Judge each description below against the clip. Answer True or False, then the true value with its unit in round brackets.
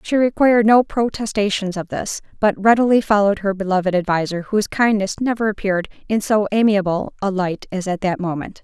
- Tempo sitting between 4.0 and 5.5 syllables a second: False (5.8 syllables/s)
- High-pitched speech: True (205 Hz)